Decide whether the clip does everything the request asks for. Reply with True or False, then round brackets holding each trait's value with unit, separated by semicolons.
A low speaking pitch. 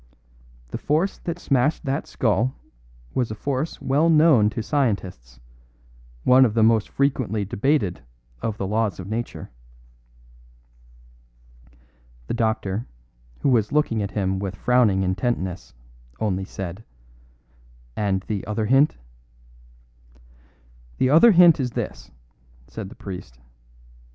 True (110 Hz)